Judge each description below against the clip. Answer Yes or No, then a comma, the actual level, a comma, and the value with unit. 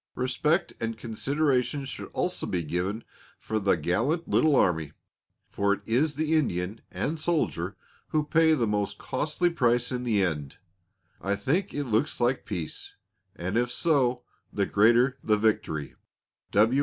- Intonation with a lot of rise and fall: Yes, wide, 6.5 semitones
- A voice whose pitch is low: Yes, low, 120 Hz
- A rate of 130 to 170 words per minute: Yes, average, 145 wpm